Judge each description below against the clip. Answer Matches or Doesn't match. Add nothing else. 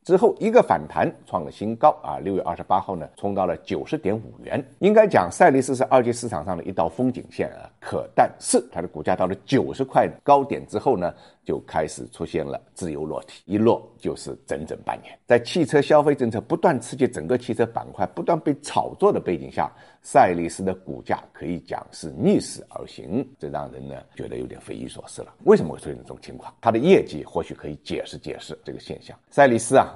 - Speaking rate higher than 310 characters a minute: Matches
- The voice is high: Doesn't match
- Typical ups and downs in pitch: Doesn't match